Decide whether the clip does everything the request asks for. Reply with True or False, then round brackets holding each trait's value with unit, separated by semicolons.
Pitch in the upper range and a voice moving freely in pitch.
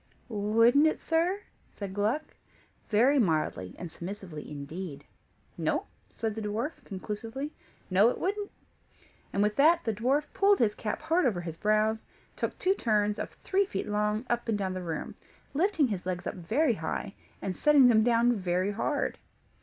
True (215 Hz; 6.4 semitones)